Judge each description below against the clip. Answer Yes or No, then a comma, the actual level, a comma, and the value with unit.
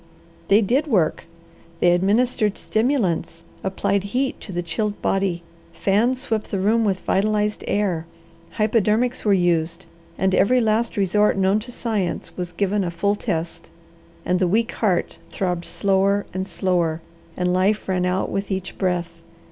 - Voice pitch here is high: Yes, high, 195 Hz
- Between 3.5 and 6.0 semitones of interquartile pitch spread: No, average, 3.0 semitones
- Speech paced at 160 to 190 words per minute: No, average, 150 wpm